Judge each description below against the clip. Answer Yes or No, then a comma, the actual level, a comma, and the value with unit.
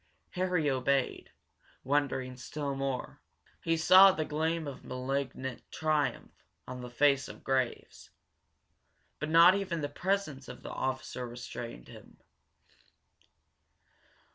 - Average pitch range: Yes, average, 3.7 semitones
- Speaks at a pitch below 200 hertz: Yes, medium, 140 Hz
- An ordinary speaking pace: No, slow, 115 wpm